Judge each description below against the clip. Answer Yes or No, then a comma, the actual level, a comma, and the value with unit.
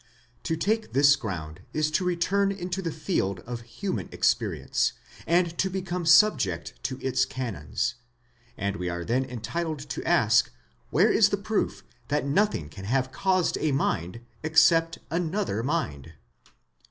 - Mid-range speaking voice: Yes, medium, 150 Hz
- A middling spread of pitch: No, wide, 7.7 semitones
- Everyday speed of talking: Yes, average, 145 wpm